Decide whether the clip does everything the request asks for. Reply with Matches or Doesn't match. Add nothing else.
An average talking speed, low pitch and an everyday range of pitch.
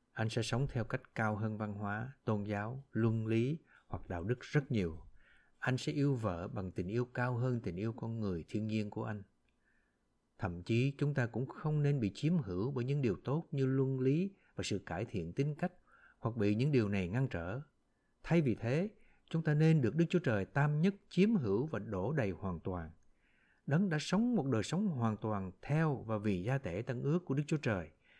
Doesn't match